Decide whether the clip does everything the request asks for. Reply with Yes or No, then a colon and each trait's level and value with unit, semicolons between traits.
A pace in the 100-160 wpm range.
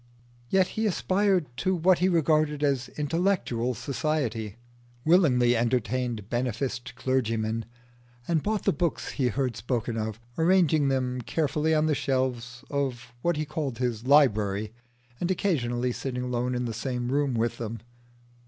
Yes: average, 145 wpm